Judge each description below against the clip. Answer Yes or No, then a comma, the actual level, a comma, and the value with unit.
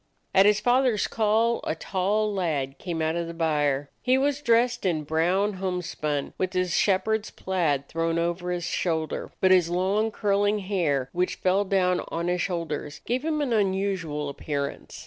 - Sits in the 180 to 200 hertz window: Yes, medium, 185 Hz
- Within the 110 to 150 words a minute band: No, average, 170 wpm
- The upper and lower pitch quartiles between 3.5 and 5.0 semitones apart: Yes, average, 4.1 semitones